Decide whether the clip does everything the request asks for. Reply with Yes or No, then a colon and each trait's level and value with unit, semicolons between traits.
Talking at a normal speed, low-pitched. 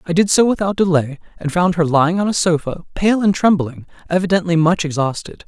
No: average, 195 wpm; medium, 175 Hz